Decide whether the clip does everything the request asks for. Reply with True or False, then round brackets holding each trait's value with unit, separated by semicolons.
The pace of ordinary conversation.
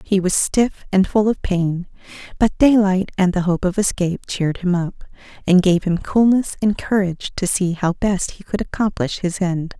True (195 wpm)